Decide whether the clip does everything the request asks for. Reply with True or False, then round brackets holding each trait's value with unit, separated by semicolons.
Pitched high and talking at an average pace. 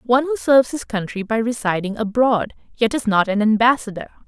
True (230 Hz; 180 wpm)